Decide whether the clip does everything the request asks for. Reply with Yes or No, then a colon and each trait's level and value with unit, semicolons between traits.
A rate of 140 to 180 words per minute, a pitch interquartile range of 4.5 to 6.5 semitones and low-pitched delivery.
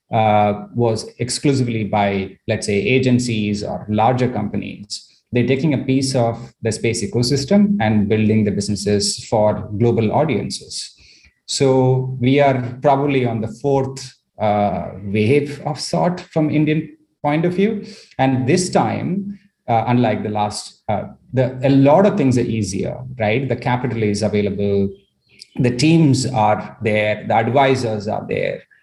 Yes: average, 145 wpm; average, 4.9 semitones; low, 120 Hz